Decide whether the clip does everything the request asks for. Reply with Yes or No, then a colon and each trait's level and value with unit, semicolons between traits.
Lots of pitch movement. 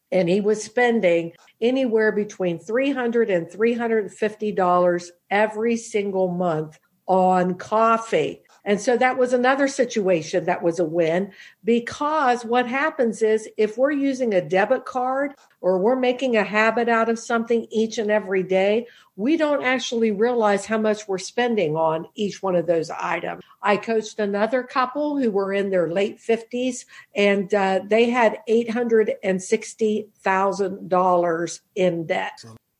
No: average, 4.2 semitones